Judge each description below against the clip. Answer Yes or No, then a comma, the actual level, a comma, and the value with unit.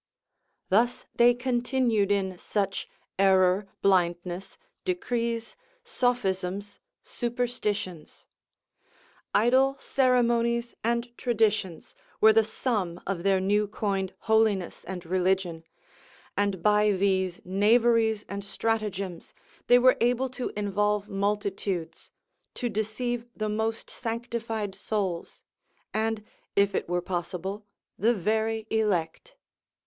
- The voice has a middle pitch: No, high, 210 Hz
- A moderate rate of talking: No, slow, 100 wpm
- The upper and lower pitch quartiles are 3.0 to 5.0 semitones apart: Yes, average, 3.5 semitones